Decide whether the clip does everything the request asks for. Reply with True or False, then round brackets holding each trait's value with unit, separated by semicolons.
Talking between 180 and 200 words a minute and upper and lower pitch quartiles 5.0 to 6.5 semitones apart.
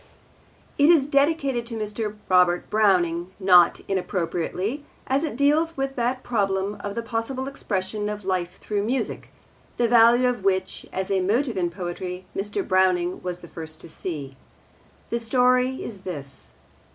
False (150 wpm; 5.3 semitones)